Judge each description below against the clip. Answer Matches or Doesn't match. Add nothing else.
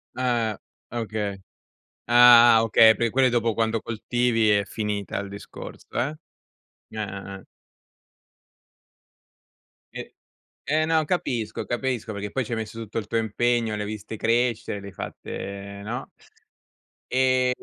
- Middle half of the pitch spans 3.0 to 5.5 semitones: Doesn't match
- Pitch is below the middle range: Matches